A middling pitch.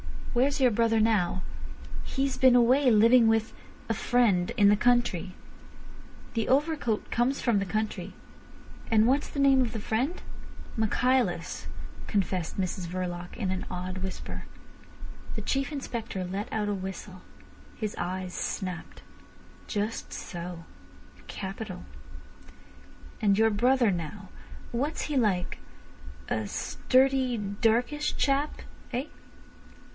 No: high, 220 Hz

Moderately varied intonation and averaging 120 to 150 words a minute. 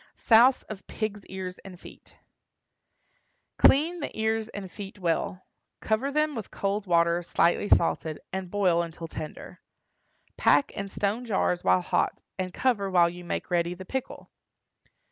Yes: average, 3.9 semitones; average, 145 wpm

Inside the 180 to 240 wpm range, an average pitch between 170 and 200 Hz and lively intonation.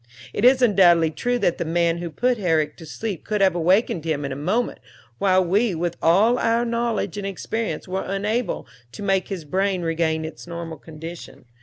No: average, 190 wpm; medium, 185 Hz; average, 4.4 semitones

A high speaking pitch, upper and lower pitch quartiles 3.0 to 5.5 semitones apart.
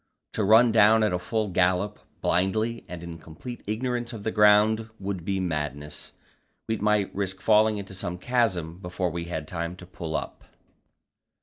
No: low, 100 Hz; average, 3.7 semitones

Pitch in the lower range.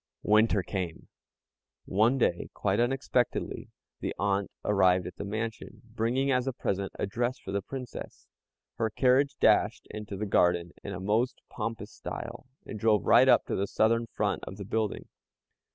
Yes: low, 110 Hz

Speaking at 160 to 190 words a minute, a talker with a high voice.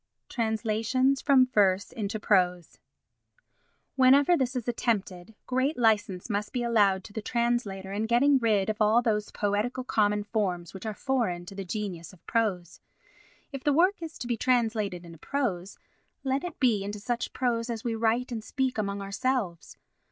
Yes: average, 165 wpm; high, 220 Hz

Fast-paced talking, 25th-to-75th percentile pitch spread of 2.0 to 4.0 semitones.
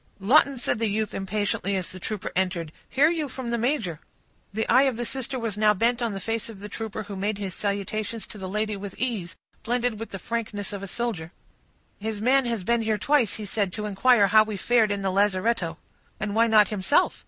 Yes: fast, 220 wpm; average, 2.9 semitones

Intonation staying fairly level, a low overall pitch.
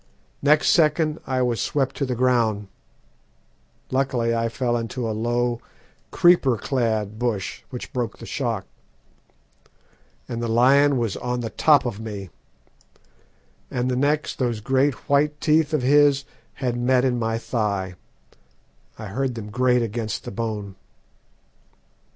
No: average, 3.1 semitones; low, 120 Hz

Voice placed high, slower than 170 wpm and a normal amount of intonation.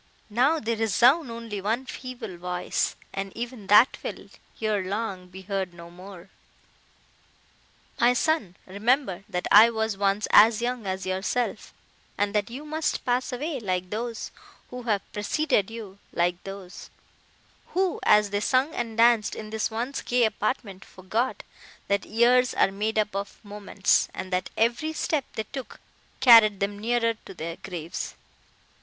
Yes: high, 215 Hz; average, 150 wpm; average, 3.7 semitones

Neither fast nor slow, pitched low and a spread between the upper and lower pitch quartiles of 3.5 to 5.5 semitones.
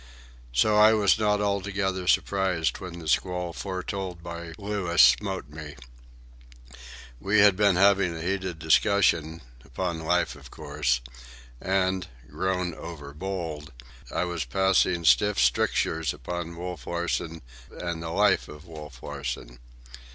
No: slow, 120 wpm; very low, 85 Hz; average, 3.8 semitones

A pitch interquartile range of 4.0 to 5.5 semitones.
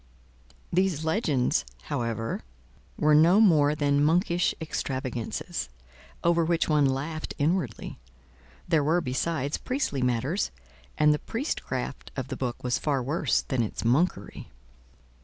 Yes: average, 4.4 semitones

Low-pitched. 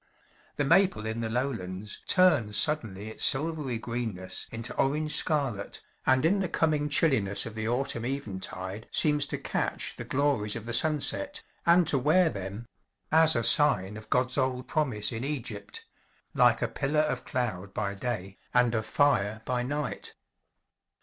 Yes: low, 125 Hz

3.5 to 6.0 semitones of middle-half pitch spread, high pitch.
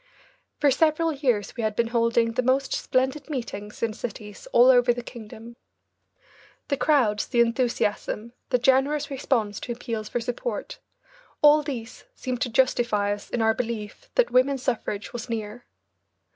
No: average, 2.8 semitones; high, 240 Hz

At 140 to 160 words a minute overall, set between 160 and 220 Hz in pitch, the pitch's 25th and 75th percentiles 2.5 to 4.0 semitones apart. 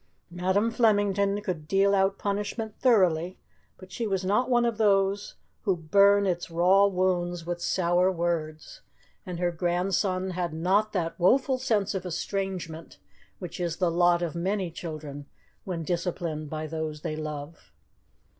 Yes: average, 145 wpm; medium, 185 Hz; average, 2.9 semitones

